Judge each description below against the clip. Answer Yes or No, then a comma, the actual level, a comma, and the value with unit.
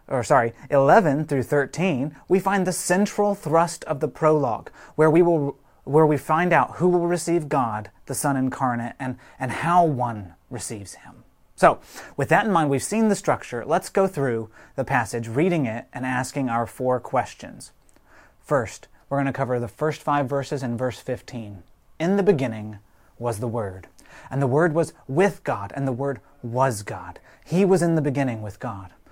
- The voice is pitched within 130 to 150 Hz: Yes, medium, 140 Hz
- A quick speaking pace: No, average, 185 wpm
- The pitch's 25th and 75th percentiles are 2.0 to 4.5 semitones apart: No, average, 5.0 semitones